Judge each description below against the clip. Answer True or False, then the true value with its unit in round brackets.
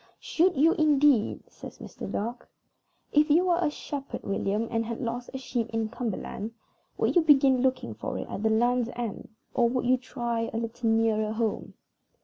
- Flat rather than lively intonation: False (3.2 semitones)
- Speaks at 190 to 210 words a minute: False (180 wpm)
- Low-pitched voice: False (240 Hz)